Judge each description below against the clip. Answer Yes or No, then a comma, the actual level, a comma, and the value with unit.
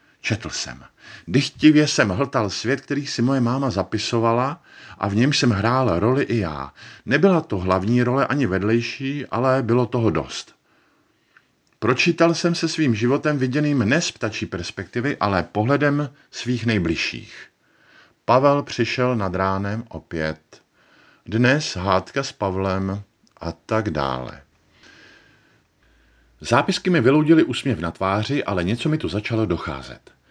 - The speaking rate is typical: Yes, average, 135 wpm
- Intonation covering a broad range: Yes, wide, 5.9 semitones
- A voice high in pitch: No, low, 120 Hz